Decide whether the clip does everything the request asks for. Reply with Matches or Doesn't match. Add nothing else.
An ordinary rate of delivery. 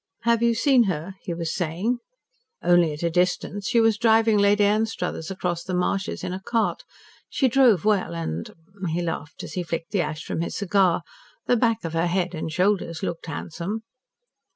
Matches